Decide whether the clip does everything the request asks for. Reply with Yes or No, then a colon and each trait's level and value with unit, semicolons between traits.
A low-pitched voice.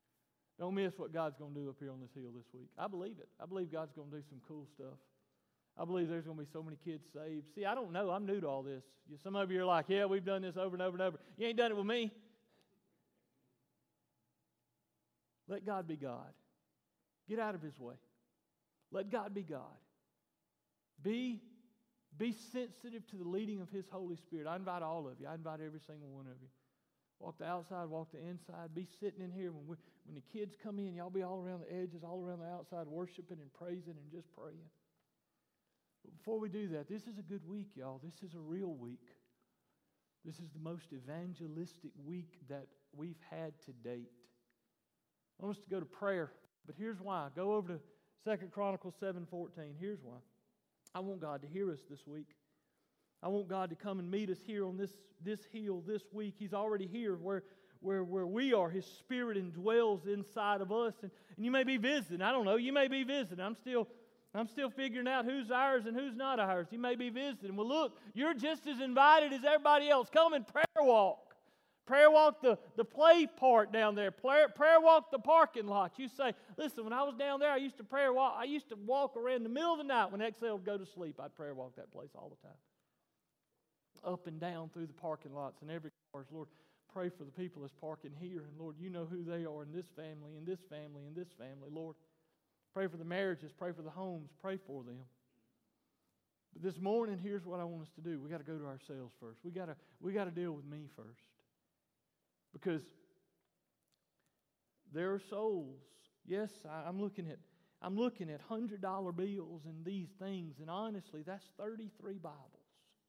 No: medium, 185 Hz